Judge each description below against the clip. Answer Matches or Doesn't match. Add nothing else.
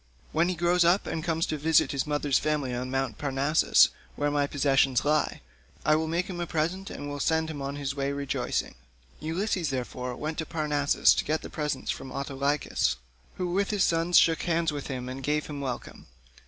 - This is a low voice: Doesn't match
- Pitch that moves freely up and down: Doesn't match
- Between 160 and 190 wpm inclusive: Doesn't match